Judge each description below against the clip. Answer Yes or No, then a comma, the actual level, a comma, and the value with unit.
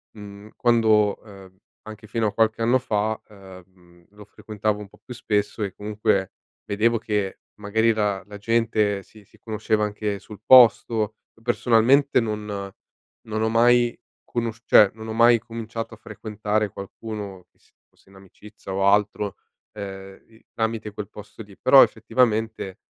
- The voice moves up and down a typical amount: No, narrow, 1.8 semitones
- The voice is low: Yes, low, 105 Hz